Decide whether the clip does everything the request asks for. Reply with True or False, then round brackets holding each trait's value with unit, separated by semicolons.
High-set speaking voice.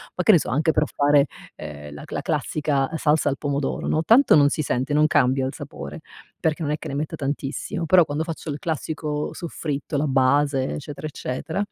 False (145 Hz)